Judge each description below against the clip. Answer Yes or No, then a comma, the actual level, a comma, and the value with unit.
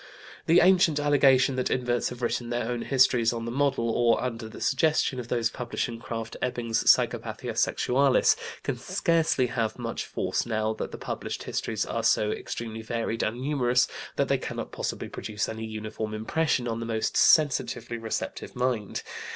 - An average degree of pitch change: No, narrow, 2.3 semitones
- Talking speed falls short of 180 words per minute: Yes, average, 170 wpm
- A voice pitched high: No, low, 120 Hz